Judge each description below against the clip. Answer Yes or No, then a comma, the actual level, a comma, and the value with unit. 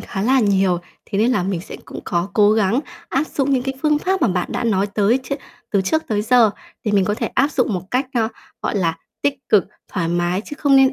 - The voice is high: Yes, high, 215 Hz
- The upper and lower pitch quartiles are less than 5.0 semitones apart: No, wide, 5.4 semitones